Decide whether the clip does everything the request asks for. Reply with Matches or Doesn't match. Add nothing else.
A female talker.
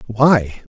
Doesn't match